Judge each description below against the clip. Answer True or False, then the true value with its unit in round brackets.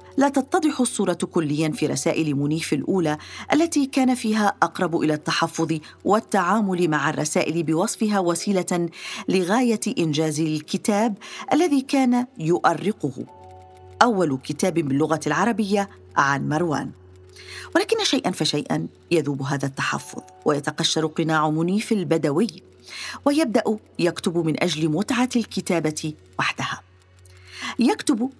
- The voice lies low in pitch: False (170 Hz)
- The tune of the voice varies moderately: False (6.1 semitones)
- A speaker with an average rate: True (105 wpm)